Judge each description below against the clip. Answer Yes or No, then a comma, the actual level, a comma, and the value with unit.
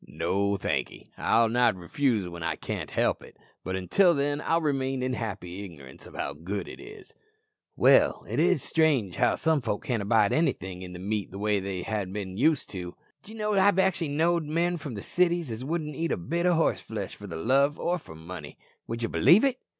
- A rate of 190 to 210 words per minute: Yes, average, 200 wpm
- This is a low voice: Yes, low, 120 Hz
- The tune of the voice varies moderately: No, wide, 9.0 semitones